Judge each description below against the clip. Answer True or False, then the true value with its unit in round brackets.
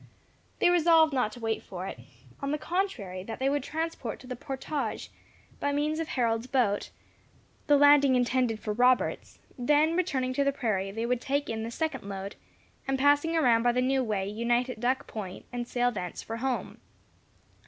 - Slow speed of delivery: False (185 wpm)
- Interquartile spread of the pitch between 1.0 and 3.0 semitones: False (4.2 semitones)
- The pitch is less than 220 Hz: False (255 Hz)